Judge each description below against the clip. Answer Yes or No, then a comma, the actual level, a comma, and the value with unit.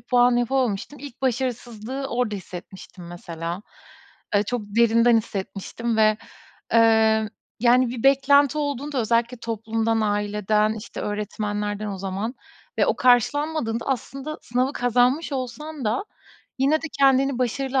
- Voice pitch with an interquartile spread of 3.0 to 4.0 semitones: Yes, average, 3.7 semitones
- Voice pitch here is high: Yes, high, 235 Hz